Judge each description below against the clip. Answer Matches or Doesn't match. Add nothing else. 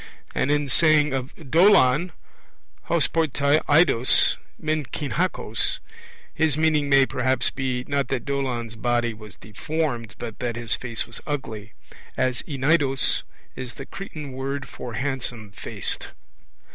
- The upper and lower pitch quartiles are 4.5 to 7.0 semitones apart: Doesn't match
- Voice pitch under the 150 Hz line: Matches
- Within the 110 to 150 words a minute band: Matches